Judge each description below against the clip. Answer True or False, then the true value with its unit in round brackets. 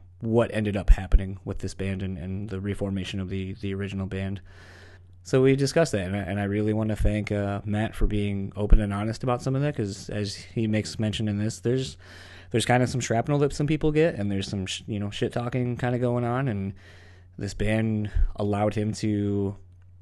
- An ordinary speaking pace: False (220 wpm)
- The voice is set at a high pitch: False (105 Hz)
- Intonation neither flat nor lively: True (3.0 semitones)